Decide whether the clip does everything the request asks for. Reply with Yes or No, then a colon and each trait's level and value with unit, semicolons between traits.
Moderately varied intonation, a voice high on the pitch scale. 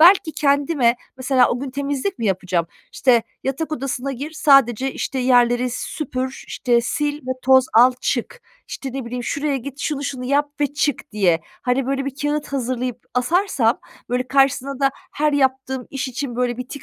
No: narrow, 2.3 semitones; very high, 265 Hz